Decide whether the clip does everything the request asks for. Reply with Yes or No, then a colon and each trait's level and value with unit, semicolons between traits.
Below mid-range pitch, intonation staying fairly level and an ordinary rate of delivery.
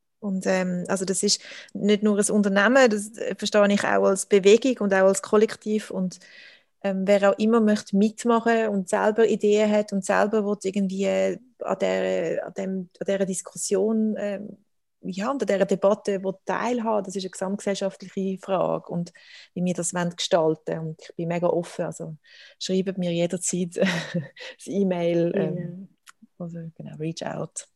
No: high, 195 Hz; narrow, 2.3 semitones; average, 155 wpm